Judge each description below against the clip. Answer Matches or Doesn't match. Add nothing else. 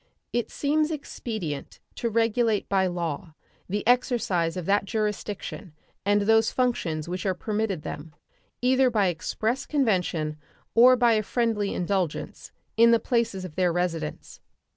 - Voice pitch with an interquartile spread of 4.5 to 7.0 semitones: Matches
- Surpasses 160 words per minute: Doesn't match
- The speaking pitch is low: Doesn't match